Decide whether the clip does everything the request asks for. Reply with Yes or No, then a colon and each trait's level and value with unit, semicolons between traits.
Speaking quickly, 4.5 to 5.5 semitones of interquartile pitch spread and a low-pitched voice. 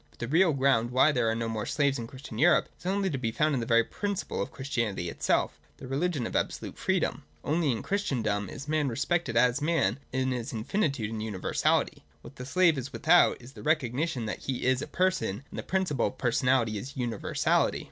Yes: fast, 210 wpm; average, 5.0 semitones; low, 130 Hz